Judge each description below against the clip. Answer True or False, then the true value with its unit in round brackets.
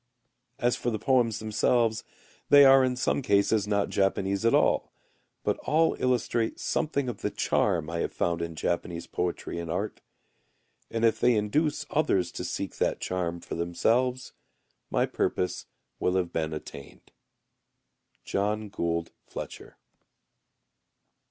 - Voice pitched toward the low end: True (105 Hz)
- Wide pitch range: True (6.1 semitones)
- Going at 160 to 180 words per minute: False (140 wpm)